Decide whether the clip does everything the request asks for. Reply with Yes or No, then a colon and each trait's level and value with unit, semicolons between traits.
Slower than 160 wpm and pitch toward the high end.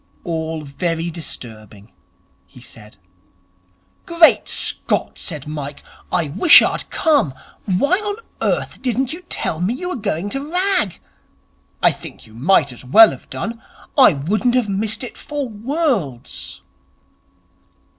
Yes: slow, 135 wpm; high, 195 Hz